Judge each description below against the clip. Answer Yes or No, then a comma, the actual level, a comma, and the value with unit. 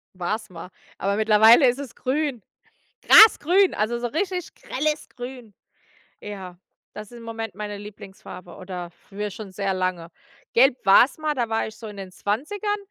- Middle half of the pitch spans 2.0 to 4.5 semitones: No, average, 5.1 semitones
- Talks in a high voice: Yes, high, 220 Hz